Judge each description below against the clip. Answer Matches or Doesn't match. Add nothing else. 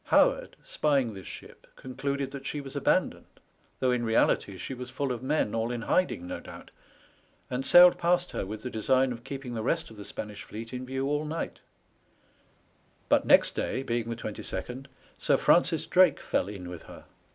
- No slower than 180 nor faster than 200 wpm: Matches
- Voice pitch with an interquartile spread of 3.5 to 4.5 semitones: Matches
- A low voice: Matches